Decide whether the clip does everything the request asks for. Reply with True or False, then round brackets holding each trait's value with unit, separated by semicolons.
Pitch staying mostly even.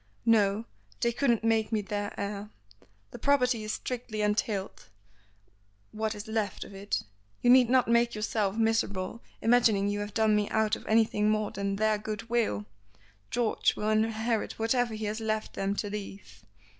True (1.8 semitones)